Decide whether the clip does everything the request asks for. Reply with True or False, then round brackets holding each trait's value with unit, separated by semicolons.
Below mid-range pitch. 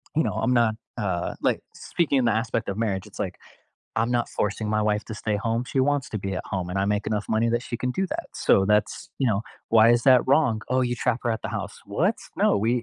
True (115 Hz)